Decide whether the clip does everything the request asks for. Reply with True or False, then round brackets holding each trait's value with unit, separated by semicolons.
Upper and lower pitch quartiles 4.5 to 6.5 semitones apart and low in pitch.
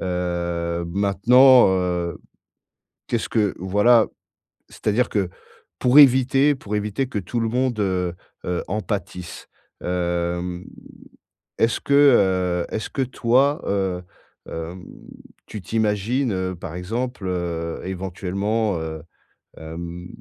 True (4.8 semitones; 95 Hz)